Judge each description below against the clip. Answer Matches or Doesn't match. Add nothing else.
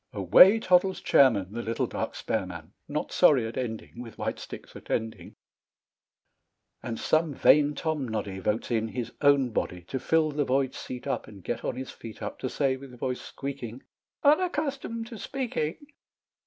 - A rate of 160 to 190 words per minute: Matches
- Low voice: Matches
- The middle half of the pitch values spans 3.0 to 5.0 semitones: Doesn't match